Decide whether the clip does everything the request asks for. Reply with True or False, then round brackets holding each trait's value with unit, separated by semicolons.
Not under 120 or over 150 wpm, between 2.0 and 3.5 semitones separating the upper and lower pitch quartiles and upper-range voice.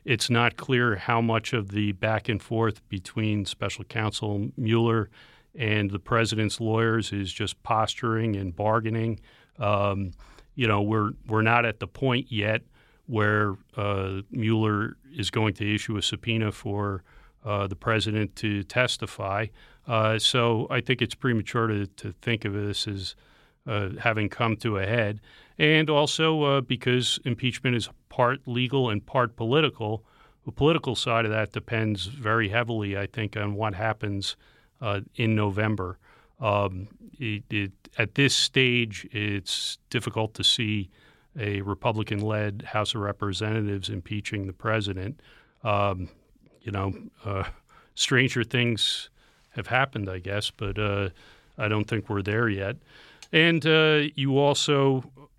False (145 wpm; 2.9 semitones; 110 Hz)